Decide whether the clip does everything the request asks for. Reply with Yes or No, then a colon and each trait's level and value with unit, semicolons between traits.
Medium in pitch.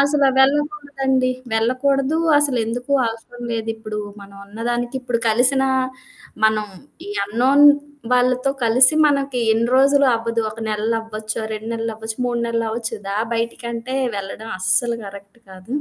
No: high, 235 Hz